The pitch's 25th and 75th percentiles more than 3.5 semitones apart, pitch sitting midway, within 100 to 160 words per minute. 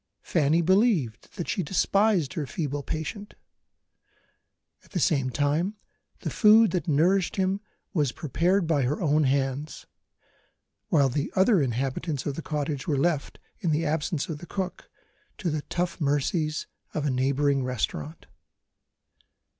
Yes: average, 4.1 semitones; medium, 155 Hz; average, 140 wpm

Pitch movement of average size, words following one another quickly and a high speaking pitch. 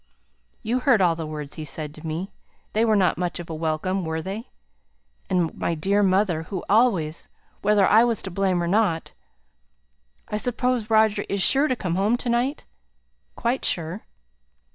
No: average, 4.9 semitones; average, 175 wpm; high, 195 Hz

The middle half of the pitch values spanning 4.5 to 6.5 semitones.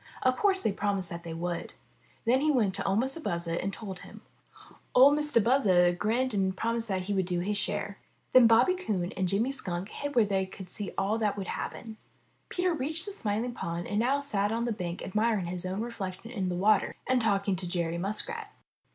Yes: average, 4.8 semitones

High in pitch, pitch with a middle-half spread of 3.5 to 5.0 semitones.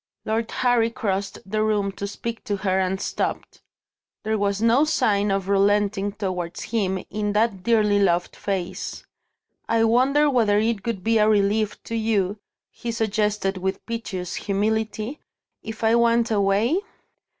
No: high, 210 Hz; narrow, 2.4 semitones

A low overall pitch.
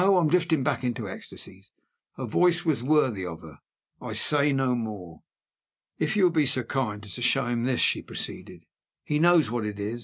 Yes: low, 130 Hz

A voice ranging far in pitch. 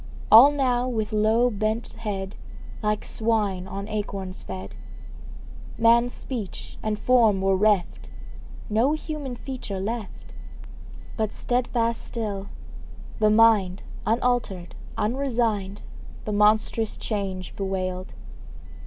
No: average, 3.2 semitones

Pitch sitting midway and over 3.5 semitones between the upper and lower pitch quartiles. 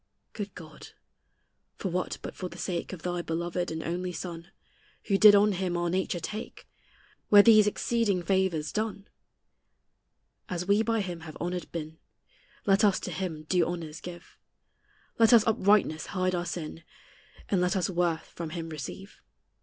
No: medium, 180 Hz; average, 2.9 semitones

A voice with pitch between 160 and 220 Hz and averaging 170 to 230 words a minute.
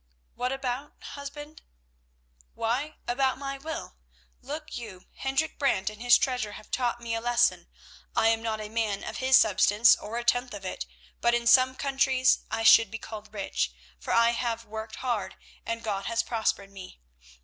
No: high, 235 Hz; average, 175 wpm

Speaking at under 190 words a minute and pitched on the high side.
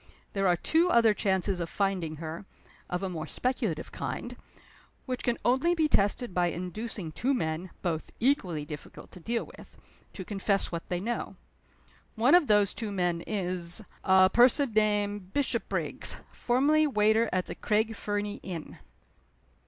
Yes: average, 150 wpm; high, 205 Hz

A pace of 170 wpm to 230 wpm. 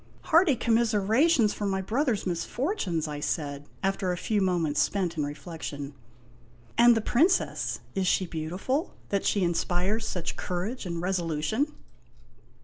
No: average, 145 wpm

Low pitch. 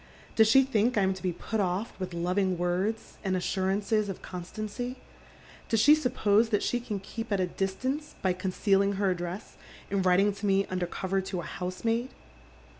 No: high, 195 Hz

